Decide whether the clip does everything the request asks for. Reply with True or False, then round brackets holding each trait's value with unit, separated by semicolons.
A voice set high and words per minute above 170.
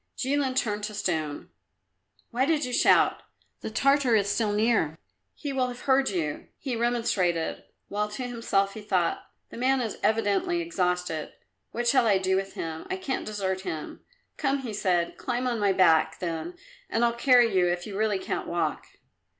True (215 Hz; 180 wpm)